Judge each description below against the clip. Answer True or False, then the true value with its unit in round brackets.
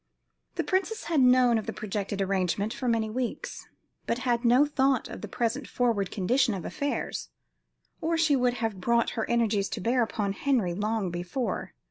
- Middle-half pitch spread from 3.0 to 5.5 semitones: True (3.8 semitones)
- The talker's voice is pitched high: True (235 Hz)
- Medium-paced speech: True (175 wpm)